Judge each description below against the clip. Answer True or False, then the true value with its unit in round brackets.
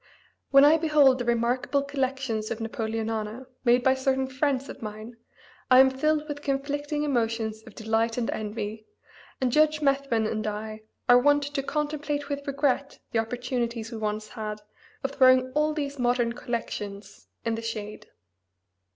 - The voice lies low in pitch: False (250 Hz)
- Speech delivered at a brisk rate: False (155 wpm)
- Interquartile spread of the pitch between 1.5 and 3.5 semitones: False (3.9 semitones)